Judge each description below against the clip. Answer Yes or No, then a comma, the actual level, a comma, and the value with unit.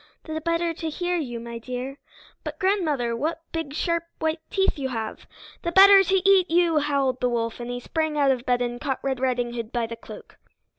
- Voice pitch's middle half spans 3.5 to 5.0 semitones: No, wide, 5.5 semitones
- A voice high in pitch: Yes, very high, 280 Hz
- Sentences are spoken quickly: Yes, fast, 210 wpm